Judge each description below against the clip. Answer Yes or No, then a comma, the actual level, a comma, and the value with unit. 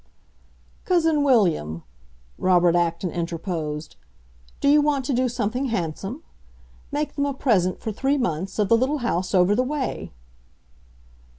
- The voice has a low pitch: No, high, 220 Hz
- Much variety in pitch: Yes, wide, 7.9 semitones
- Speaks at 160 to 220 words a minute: No, slow, 135 wpm